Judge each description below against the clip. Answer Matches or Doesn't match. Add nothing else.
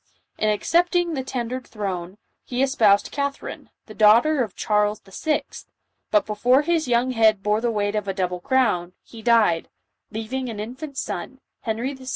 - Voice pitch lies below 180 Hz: Doesn't match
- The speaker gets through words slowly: Doesn't match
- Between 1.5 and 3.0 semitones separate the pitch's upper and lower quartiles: Doesn't match